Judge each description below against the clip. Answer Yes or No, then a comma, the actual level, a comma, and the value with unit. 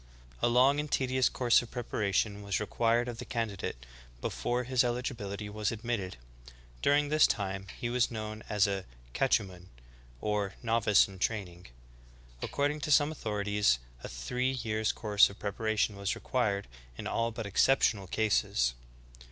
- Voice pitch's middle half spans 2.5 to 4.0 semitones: Yes, average, 3.5 semitones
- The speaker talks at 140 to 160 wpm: Yes, average, 145 wpm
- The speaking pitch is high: No, low, 110 Hz